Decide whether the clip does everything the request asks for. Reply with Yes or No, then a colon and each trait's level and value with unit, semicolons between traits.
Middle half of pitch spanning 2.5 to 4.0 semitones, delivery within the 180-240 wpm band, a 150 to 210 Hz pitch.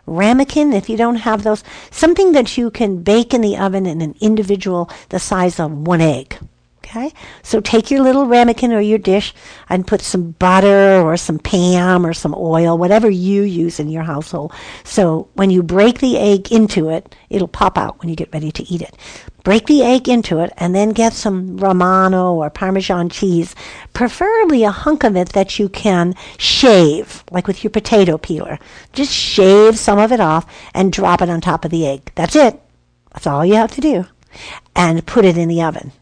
No: average, 4.6 semitones; average, 200 wpm; high, 190 Hz